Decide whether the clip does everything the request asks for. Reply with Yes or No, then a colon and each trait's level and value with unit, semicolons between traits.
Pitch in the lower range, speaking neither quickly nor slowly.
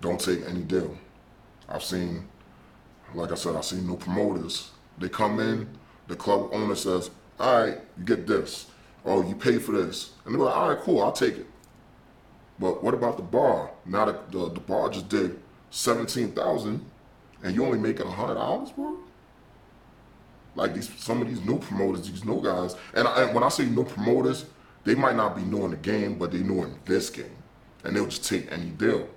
Yes: very low, 90 Hz; average, 195 wpm